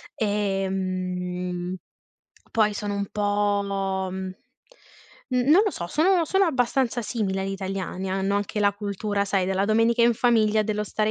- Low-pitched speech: No, high, 205 Hz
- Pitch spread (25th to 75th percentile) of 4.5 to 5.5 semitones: No, narrow, 2.5 semitones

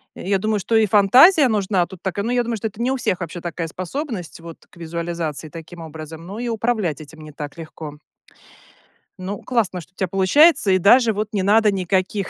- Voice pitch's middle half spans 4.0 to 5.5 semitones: Yes, average, 4.6 semitones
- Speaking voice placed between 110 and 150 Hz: No, high, 190 Hz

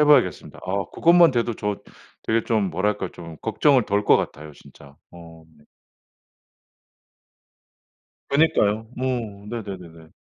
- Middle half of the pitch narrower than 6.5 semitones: Yes, wide, 5.4 semitones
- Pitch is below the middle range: Yes, low, 105 Hz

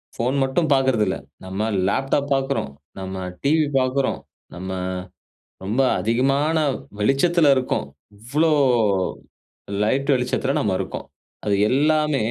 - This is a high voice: No, low, 135 Hz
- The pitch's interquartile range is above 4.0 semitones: Yes, average, 4.7 semitones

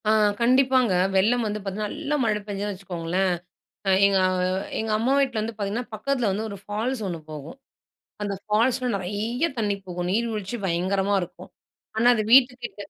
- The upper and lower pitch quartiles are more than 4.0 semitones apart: No, average, 3.6 semitones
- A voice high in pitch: Yes, high, 210 Hz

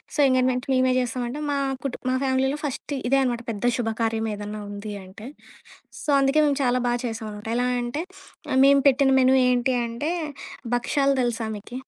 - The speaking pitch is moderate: No, very high, 250 Hz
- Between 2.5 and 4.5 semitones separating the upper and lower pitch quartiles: Yes, average, 2.8 semitones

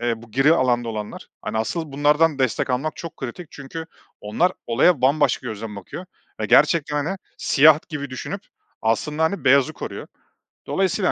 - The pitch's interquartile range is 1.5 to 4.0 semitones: No, average, 5.1 semitones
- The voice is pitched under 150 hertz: Yes, medium, 140 Hz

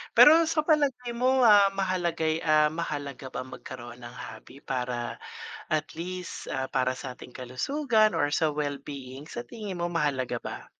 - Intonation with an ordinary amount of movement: No, wide, 8.1 semitones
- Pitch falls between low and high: Yes, medium, 155 Hz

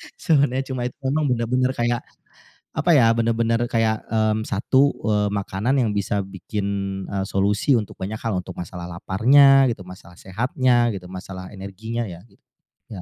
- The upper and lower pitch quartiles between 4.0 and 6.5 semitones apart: Yes, average, 4.3 semitones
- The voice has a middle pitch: No, low, 110 Hz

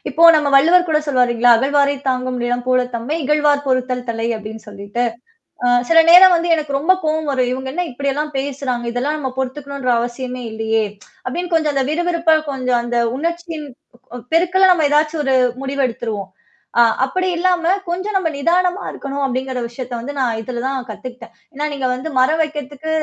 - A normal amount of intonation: Yes, average, 3.9 semitones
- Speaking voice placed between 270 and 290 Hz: Yes, very high, 275 Hz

